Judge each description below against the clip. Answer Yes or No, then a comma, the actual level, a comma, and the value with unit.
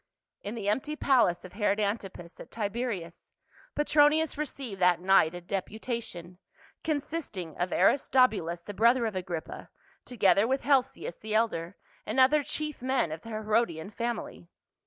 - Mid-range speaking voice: No, high, 215 Hz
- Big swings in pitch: Yes, wide, 6.2 semitones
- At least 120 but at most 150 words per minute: Yes, average, 140 wpm